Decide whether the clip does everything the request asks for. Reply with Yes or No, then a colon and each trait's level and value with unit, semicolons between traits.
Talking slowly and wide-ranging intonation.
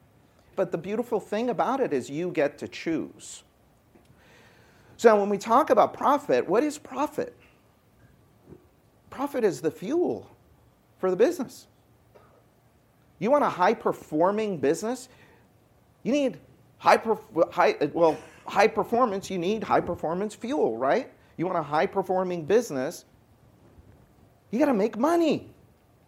Yes: slow, 125 wpm; wide, 7.1 semitones